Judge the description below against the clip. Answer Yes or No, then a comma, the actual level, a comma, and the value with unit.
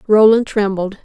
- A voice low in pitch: No, high, 210 Hz